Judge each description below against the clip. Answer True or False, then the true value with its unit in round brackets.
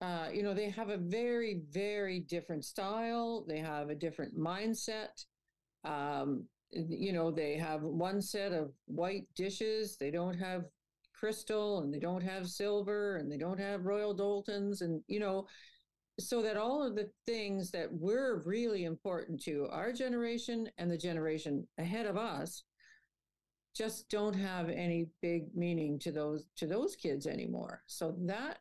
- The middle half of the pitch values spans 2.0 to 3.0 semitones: False (4.5 semitones)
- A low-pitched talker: False (195 Hz)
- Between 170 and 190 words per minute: False (160 wpm)